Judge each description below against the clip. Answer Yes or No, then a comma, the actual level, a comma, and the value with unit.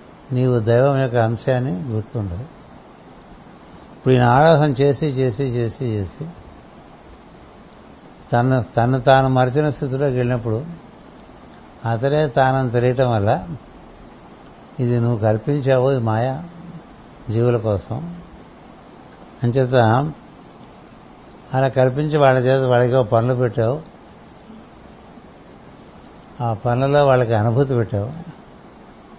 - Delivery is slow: No, average, 85 wpm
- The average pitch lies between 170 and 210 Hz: No, low, 130 Hz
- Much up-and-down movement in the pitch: No, average, 2.7 semitones